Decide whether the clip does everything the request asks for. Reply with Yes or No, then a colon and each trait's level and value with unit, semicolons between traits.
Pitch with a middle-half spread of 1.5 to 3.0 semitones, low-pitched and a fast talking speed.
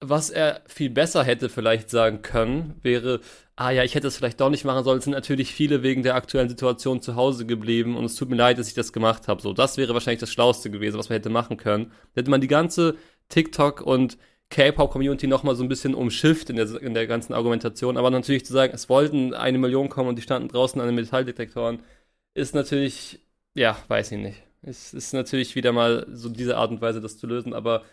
Yes: narrow, 2.6 semitones; low, 125 Hz; fast, 230 wpm